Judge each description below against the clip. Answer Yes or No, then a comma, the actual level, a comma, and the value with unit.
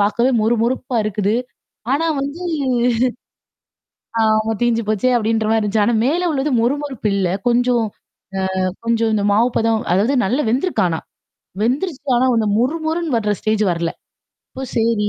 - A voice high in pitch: Yes, high, 230 Hz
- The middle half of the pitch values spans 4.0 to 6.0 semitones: No, average, 3.3 semitones